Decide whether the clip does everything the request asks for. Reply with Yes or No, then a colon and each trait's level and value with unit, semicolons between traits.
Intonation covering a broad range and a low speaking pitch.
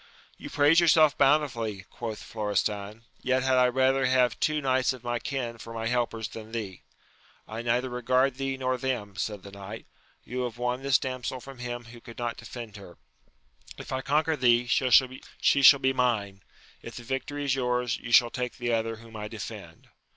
No: narrow, 2.6 semitones; low, 125 Hz